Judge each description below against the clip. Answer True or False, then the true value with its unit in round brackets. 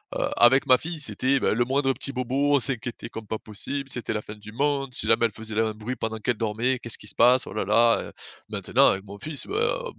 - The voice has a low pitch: True (120 Hz)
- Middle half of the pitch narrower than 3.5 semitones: False (3.8 semitones)